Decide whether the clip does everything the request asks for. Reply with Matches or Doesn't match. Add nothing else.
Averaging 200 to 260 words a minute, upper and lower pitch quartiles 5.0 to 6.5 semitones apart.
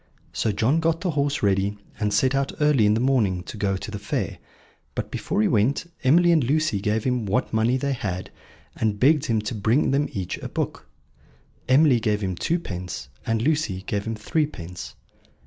Doesn't match